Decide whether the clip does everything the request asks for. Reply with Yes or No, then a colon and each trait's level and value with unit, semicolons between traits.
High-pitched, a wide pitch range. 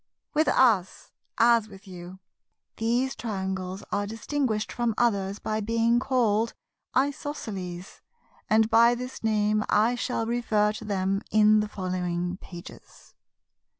No: high, 215 Hz; average, 3.3 semitones